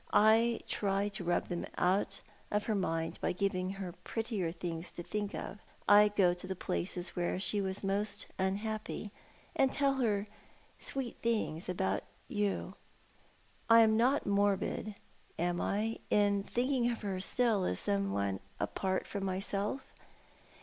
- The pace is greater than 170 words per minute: No, average, 150 wpm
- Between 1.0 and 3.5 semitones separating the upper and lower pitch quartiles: Yes, average, 2.8 semitones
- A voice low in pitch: No, high, 200 Hz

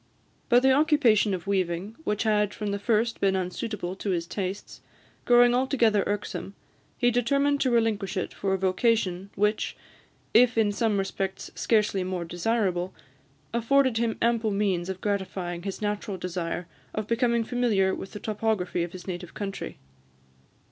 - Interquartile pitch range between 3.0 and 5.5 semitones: Yes, average, 3.5 semitones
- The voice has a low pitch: No, high, 205 Hz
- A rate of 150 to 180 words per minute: Yes, average, 155 wpm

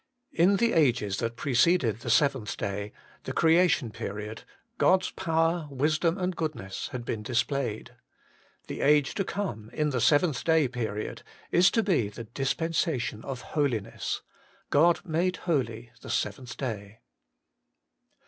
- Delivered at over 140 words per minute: No, slow, 135 wpm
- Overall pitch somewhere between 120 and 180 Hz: Yes, low, 135 Hz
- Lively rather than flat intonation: Yes, wide, 6.2 semitones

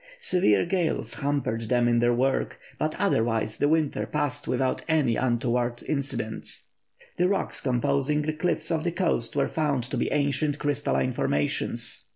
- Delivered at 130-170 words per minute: Yes, average, 155 wpm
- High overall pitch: No, medium, 140 Hz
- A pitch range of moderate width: Yes, average, 4.3 semitones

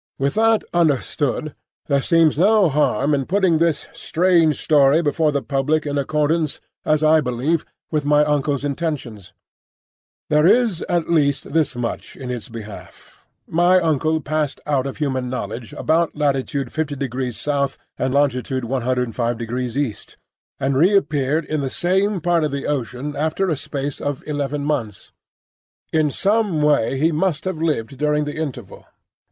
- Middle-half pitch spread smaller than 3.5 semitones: Yes, average, 3.0 semitones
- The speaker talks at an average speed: Yes, average, 150 wpm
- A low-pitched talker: No, medium, 145 Hz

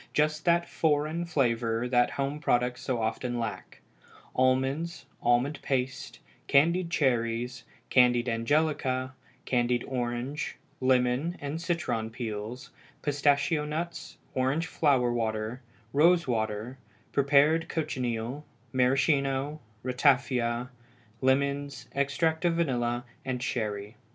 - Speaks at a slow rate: Yes, slow, 100 wpm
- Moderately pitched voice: No, low, 130 Hz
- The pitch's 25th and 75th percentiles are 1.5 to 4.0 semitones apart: Yes, average, 3.5 semitones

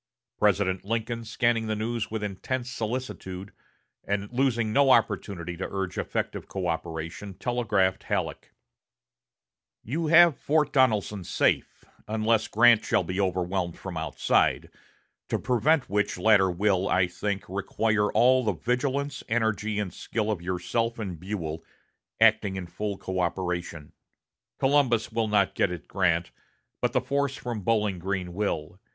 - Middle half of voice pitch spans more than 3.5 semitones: Yes, average, 4.0 semitones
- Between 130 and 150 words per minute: Yes, slow, 135 wpm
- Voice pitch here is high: No, low, 105 Hz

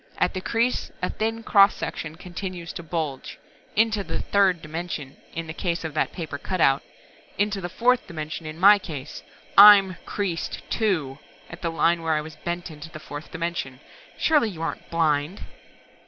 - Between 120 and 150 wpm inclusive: No, average, 170 wpm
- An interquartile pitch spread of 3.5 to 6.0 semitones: Yes, average, 4.0 semitones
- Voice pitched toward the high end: No, medium, 170 Hz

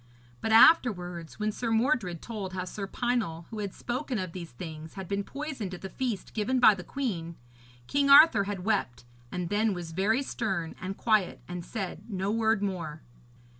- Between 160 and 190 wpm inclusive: Yes, average, 180 wpm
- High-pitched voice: Yes, high, 200 Hz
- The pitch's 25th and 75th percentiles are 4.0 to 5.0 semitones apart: Yes, average, 4.3 semitones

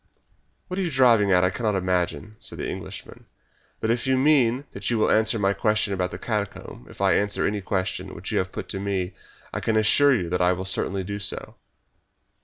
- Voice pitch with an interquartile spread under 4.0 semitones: Yes, average, 3.5 semitones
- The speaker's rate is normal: No, fast, 215 wpm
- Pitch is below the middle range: Yes, low, 100 Hz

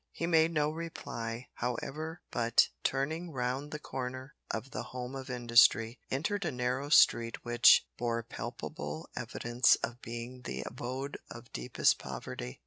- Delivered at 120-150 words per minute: Yes, average, 140 wpm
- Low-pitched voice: Yes, low, 125 Hz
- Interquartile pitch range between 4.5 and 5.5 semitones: No, average, 4.0 semitones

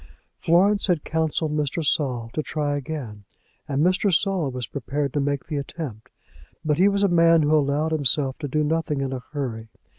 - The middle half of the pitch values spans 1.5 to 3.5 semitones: Yes, average, 3.0 semitones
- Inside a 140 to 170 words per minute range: No, average, 185 wpm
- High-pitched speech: No, medium, 150 Hz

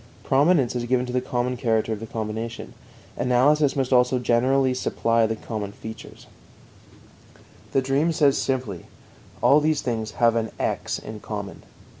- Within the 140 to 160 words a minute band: Yes, average, 150 wpm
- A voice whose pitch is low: Yes, low, 125 Hz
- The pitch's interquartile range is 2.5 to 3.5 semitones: Yes, average, 3.0 semitones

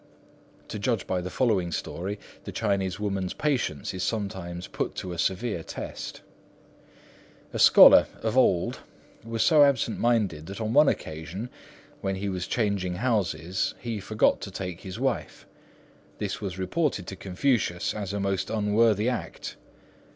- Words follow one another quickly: No, average, 150 wpm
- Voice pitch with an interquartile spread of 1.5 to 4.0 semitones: Yes, average, 3.7 semitones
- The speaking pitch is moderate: No, low, 100 Hz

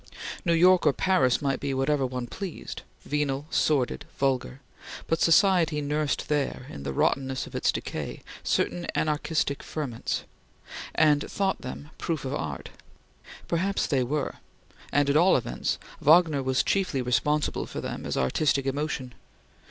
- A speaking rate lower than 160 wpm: Yes, average, 145 wpm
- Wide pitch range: No, average, 3.3 semitones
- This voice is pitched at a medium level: Yes, medium, 145 Hz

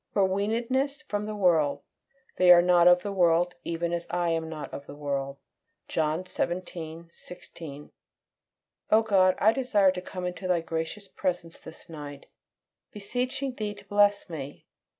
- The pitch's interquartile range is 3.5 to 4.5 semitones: Yes, average, 3.9 semitones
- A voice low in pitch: No, medium, 180 Hz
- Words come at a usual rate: Yes, average, 155 wpm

